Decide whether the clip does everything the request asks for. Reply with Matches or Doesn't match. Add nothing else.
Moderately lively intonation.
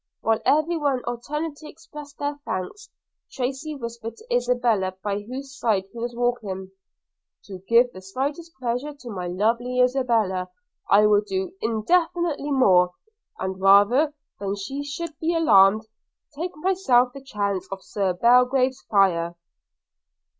Doesn't match